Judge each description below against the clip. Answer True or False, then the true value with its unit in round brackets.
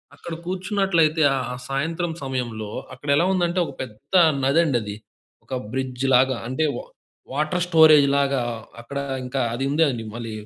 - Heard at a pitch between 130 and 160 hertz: True (140 Hz)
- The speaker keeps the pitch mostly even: False (4.1 semitones)